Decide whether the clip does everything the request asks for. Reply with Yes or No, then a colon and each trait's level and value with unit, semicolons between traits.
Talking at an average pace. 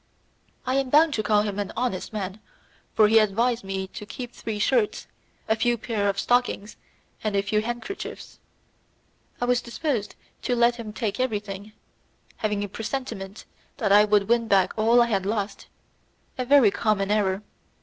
Yes: average, 170 wpm